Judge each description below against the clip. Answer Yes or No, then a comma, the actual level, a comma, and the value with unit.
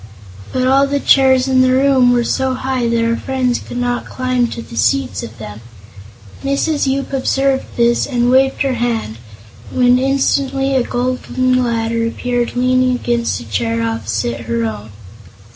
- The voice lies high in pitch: Yes, high, 245 Hz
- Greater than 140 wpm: Yes, average, 160 wpm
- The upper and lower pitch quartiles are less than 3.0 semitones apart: Yes, narrow, 2.4 semitones